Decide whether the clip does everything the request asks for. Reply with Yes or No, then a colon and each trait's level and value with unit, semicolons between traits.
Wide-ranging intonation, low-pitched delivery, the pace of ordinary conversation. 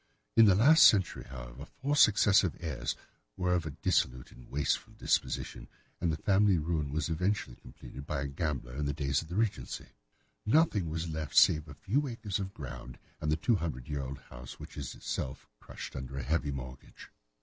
Yes: wide, 5.9 semitones; very low, 80 Hz; average, 190 wpm